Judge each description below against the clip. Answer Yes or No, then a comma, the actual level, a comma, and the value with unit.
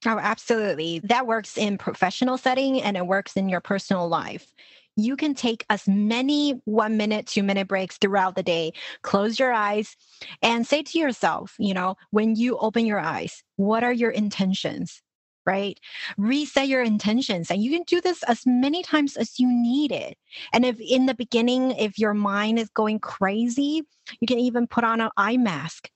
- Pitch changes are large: No, average, 3.8 semitones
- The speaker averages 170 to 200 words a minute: Yes, average, 185 wpm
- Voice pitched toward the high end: Yes, high, 225 Hz